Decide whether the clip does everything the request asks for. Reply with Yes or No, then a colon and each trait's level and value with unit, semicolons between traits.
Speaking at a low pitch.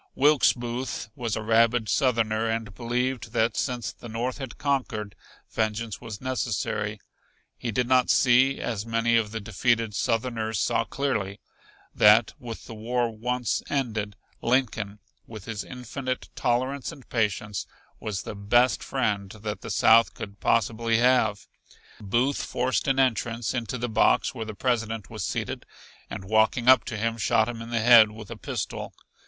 Yes: low, 115 Hz